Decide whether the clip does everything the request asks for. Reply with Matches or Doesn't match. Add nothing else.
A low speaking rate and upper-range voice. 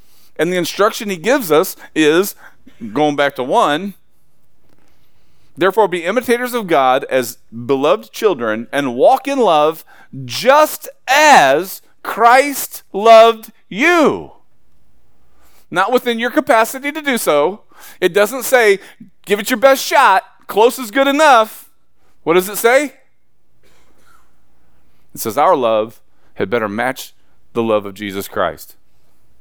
Matches